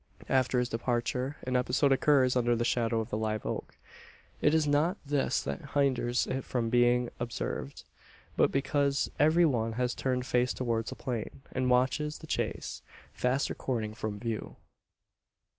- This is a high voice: No, low, 125 Hz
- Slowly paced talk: No, average, 160 wpm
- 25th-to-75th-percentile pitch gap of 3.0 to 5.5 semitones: No, narrow, 2.5 semitones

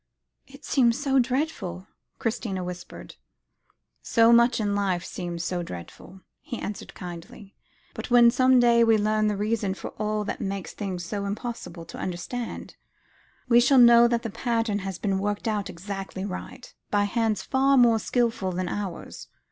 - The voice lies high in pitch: Yes, high, 210 Hz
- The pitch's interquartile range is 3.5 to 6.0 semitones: Yes, average, 3.8 semitones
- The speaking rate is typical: Yes, average, 160 wpm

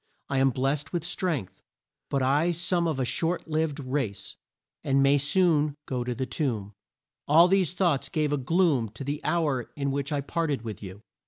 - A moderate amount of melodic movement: Yes, average, 3.8 semitones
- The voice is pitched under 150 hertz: Yes, medium, 140 Hz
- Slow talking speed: No, average, 185 wpm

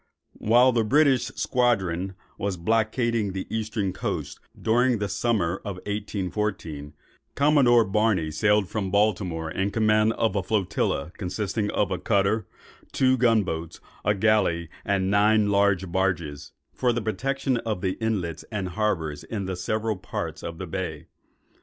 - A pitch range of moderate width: Yes, average, 3.3 semitones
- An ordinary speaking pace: Yes, average, 145 wpm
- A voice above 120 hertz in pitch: No, low, 105 Hz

